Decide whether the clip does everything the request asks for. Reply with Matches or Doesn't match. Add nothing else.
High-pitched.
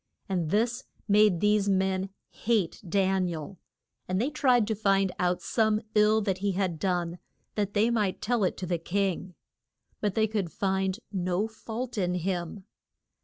Matches